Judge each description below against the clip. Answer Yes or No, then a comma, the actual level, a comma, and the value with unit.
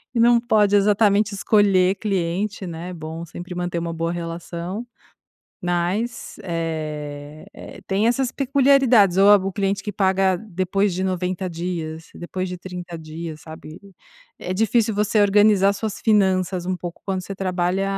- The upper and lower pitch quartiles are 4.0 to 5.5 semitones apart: No, average, 3.1 semitones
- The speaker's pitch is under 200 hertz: Yes, medium, 185 Hz